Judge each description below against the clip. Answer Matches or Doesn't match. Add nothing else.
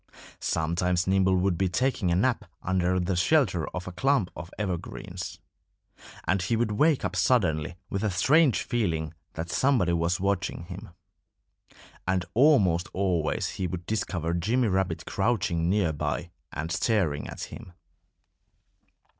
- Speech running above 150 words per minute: Doesn't match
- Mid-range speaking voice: Doesn't match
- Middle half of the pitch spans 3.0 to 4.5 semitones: Matches